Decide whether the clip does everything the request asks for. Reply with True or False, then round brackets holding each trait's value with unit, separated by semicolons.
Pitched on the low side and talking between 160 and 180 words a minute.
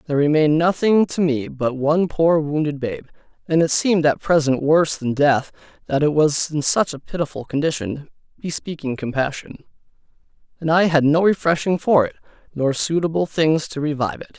False (150 Hz; 170 wpm)